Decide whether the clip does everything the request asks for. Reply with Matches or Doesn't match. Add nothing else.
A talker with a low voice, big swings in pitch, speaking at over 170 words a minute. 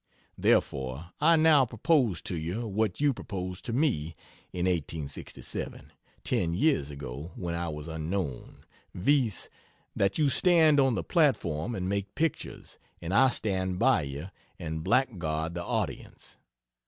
Doesn't match